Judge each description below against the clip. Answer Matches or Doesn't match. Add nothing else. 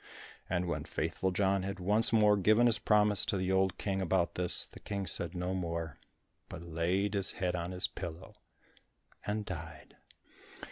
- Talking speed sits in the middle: Matches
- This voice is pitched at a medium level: Doesn't match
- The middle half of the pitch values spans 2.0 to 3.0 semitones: Matches